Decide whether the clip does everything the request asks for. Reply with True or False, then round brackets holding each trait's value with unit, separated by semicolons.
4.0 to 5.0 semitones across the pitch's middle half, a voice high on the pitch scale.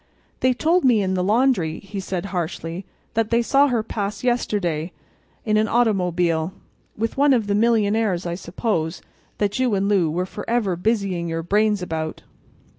True (4.3 semitones; 200 Hz)